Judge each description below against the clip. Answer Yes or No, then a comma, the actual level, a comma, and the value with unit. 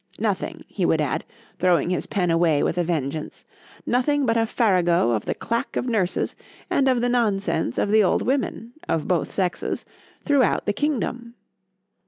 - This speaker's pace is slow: No, average, 160 wpm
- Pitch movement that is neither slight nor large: No, wide, 5.8 semitones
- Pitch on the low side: No, high, 205 Hz